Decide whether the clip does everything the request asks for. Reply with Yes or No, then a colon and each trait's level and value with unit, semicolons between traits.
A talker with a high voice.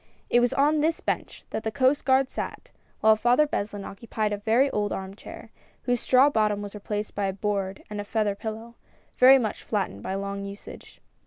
Yes: high, 215 Hz